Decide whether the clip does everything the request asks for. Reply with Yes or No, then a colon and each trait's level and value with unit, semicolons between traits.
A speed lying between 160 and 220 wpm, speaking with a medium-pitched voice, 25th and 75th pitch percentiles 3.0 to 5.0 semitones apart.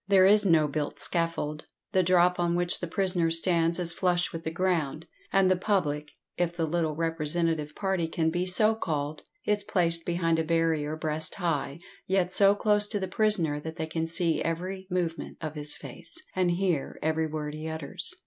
No: average, 185 wpm; medium, 170 Hz; narrow, 2.6 semitones